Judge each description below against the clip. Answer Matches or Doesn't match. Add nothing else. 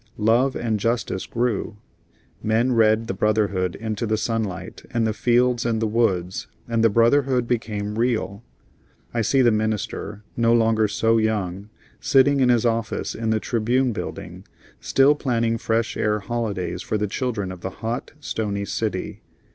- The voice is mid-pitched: Doesn't match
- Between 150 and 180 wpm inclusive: Matches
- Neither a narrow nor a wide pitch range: Doesn't match